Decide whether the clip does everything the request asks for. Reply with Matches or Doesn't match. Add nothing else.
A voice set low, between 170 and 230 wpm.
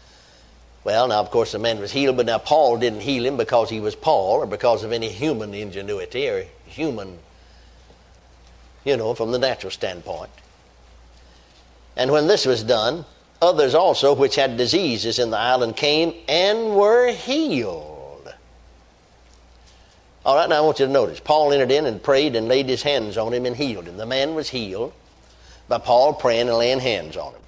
Matches